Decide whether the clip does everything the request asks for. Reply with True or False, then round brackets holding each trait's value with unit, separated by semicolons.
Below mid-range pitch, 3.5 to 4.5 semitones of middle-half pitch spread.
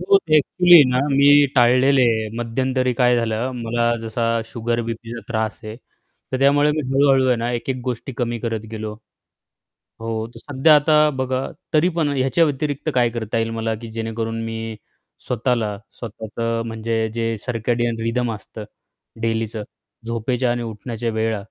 False (120 Hz; 2.7 semitones)